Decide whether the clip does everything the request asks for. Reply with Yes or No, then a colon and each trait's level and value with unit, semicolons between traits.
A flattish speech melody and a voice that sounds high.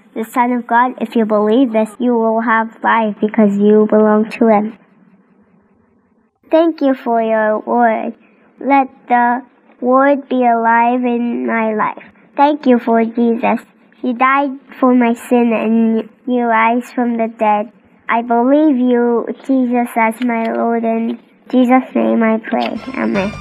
Yes: narrow, 1.9 semitones; high, 230 Hz